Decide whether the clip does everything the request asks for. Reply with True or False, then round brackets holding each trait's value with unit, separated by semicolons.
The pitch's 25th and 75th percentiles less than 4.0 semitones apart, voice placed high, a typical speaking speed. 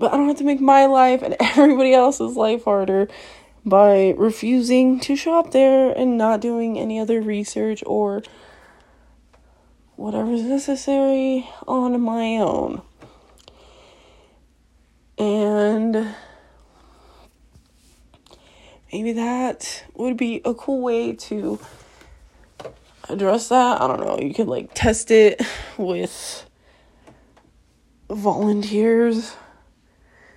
False (3.6 semitones; 230 Hz; 105 wpm)